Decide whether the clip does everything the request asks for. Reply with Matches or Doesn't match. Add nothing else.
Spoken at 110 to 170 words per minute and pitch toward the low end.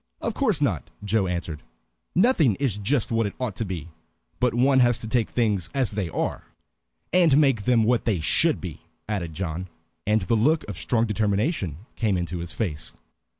Doesn't match